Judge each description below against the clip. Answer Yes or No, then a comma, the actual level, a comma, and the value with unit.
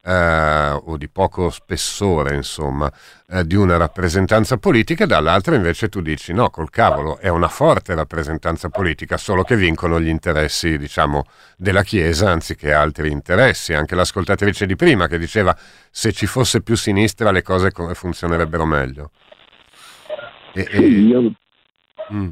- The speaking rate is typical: Yes, average, 140 wpm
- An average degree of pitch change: Yes, average, 4.2 semitones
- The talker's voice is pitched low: Yes, very low, 90 Hz